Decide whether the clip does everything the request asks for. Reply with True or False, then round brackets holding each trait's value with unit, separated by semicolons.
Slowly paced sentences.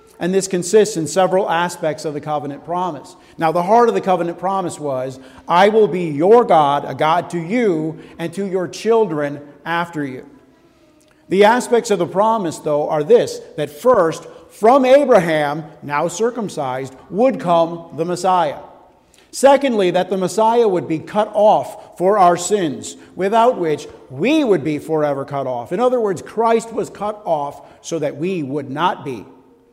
False (170 wpm)